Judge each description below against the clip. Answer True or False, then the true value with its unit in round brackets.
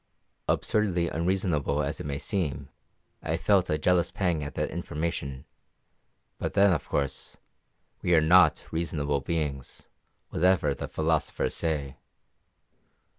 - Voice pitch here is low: True (80 Hz)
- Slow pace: True (125 wpm)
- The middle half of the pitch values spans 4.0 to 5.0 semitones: False (3.4 semitones)